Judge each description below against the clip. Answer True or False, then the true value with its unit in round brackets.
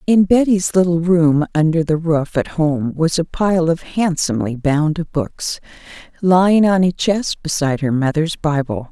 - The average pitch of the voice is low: False (165 Hz)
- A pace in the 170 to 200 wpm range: False (160 wpm)